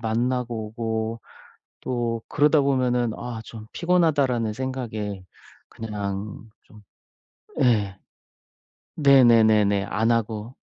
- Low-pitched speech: Yes, low, 115 Hz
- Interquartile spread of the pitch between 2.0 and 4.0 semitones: Yes, average, 2.8 semitones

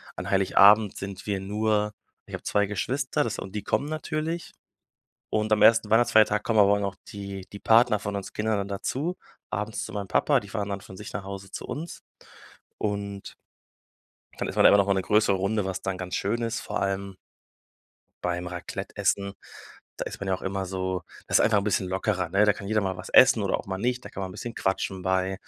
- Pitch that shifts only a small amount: Yes, narrow, 2.0 semitones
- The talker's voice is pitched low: Yes, low, 100 Hz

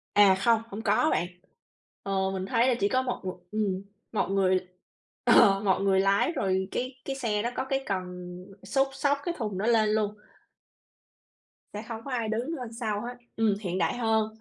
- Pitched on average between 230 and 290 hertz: No, high, 215 Hz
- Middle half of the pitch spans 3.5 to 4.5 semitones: Yes, average, 3.9 semitones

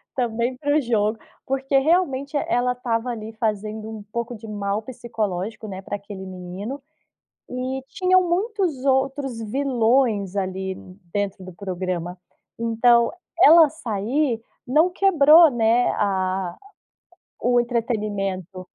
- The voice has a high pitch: Yes, high, 230 Hz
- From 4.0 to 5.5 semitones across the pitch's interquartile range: Yes, average, 4.8 semitones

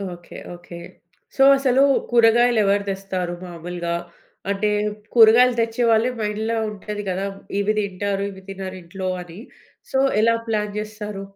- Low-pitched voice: No, high, 205 Hz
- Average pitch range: Yes, average, 3.1 semitones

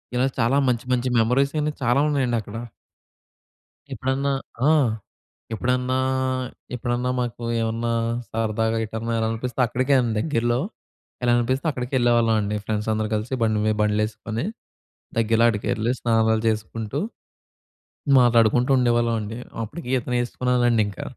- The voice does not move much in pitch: Yes, narrow, 2.0 semitones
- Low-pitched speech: Yes, low, 115 Hz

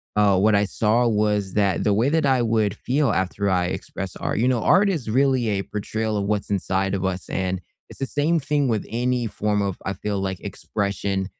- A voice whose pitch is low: Yes, low, 105 Hz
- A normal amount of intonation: Yes, average, 4.0 semitones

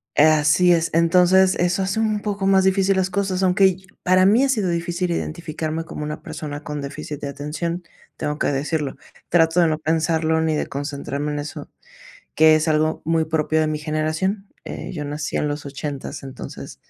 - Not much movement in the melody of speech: No, average, 3.4 semitones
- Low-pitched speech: No, medium, 160 Hz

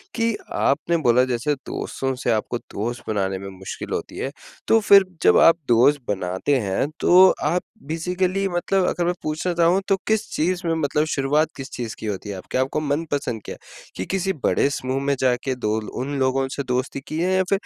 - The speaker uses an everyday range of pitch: No, wide, 6.2 semitones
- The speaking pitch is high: No, medium, 140 Hz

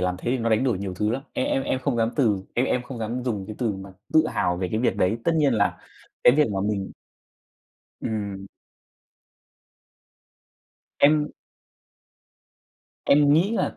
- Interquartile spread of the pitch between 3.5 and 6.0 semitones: Yes, average, 5.0 semitones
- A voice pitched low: Yes, low, 115 Hz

